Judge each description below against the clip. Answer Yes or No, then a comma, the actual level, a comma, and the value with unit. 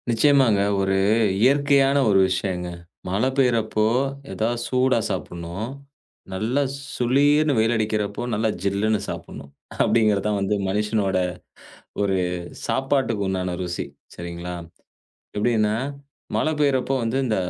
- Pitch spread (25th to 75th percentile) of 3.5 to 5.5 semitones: Yes, average, 4.7 semitones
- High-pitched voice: No, low, 110 Hz